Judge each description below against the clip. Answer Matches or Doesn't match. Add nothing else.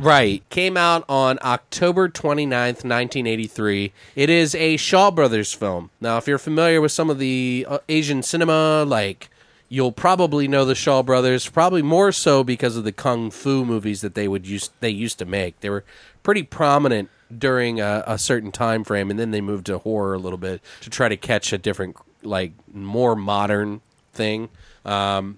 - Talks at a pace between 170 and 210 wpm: Matches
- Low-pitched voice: Matches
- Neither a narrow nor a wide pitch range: Doesn't match